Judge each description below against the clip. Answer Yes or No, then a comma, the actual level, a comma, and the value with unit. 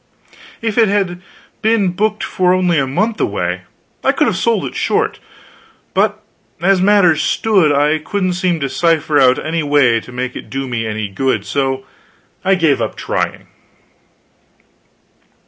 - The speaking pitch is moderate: Yes, medium, 160 Hz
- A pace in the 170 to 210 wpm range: No, average, 155 wpm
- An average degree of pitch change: No, wide, 6.1 semitones